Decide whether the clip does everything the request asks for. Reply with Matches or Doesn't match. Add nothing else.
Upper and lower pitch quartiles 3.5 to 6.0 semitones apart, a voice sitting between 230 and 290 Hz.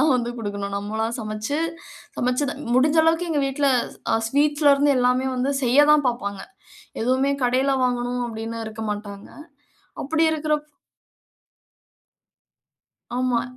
Matches